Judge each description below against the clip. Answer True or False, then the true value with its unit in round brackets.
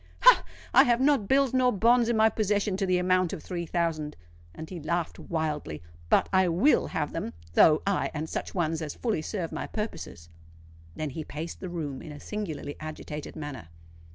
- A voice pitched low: False (170 Hz)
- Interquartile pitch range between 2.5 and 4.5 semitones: False (5.5 semitones)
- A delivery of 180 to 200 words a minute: True (185 wpm)